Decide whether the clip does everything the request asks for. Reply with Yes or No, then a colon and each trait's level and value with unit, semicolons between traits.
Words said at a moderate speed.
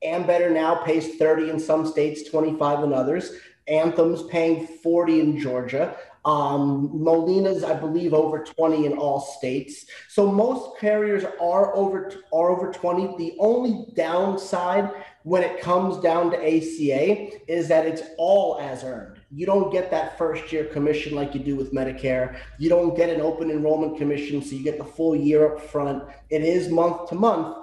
Yes: average, 175 wpm